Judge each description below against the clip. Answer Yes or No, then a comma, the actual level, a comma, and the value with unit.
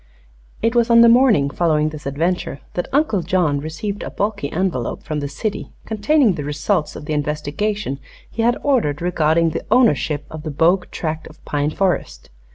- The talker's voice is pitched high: No, medium, 165 Hz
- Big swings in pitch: Yes, wide, 5.8 semitones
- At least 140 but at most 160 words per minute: No, average, 175 wpm